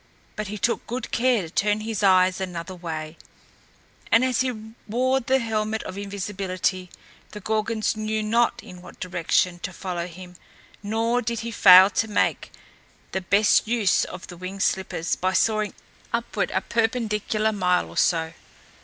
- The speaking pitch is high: Yes, high, 205 Hz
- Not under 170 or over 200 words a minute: No, average, 160 wpm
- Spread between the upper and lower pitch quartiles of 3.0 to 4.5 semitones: Yes, average, 3.5 semitones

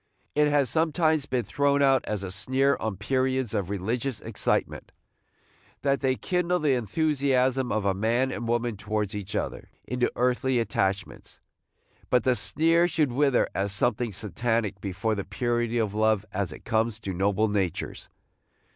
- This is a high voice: No, low, 120 Hz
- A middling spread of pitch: Yes, average, 4.5 semitones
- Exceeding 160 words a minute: No, average, 155 wpm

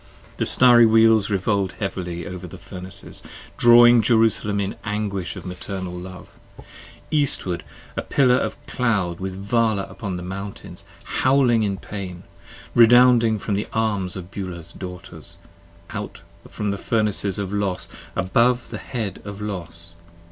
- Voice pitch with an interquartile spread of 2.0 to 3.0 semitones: No, average, 3.5 semitones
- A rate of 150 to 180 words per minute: No, average, 140 wpm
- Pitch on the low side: Yes, low, 100 Hz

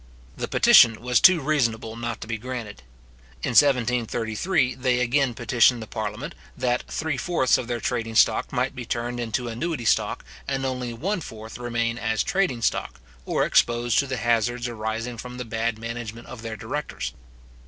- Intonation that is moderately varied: No, narrow, 2.1 semitones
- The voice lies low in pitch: Yes, low, 120 Hz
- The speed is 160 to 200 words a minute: Yes, average, 170 wpm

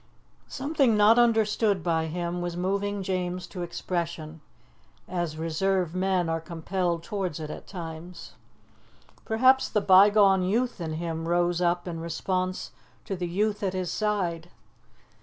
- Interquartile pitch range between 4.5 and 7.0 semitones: No, average, 3.0 semitones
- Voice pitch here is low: No, medium, 180 Hz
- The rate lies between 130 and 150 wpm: Yes, average, 140 wpm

